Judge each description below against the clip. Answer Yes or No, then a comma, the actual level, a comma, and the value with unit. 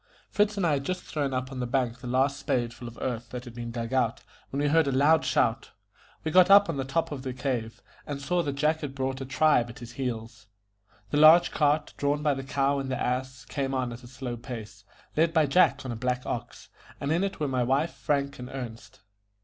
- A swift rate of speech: Yes, fast, 245 wpm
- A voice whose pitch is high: No, low, 135 Hz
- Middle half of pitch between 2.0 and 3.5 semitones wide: Yes, average, 3.1 semitones